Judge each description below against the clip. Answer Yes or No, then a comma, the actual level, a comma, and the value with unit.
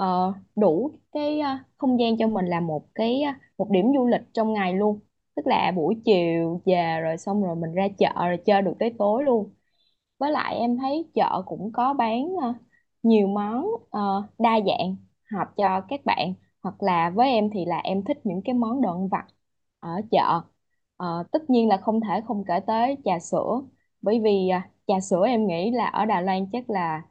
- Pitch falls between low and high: No, high, 205 Hz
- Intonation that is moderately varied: Yes, average, 4.0 semitones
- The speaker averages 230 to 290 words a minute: No, average, 210 wpm